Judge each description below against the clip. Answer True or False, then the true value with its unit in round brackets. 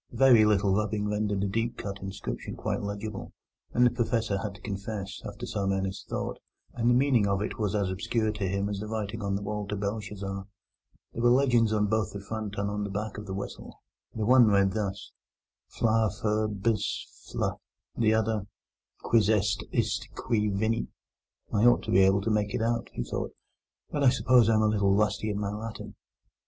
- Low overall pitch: True (105 Hz)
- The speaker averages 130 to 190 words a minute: False (205 wpm)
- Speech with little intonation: True (2.0 semitones)